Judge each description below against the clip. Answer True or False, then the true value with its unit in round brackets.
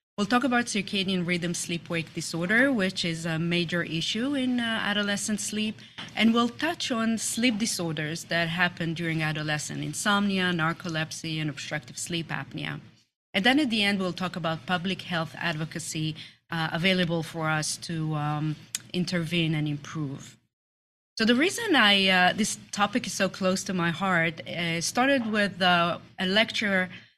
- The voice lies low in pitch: False (175 Hz)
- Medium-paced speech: True (160 wpm)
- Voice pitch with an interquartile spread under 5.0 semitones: True (4.1 semitones)